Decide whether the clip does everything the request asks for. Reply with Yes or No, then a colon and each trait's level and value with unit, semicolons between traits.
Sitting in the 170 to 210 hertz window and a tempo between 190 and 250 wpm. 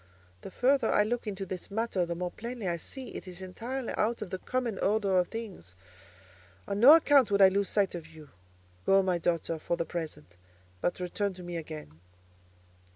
Yes: high, 190 Hz; average, 195 wpm